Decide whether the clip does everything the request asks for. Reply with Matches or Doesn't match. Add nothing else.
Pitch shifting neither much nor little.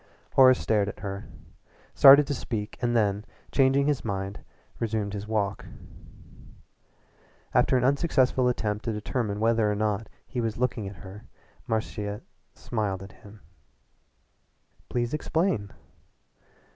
Matches